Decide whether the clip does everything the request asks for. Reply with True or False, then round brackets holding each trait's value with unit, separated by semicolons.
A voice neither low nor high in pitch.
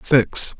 False (125 Hz)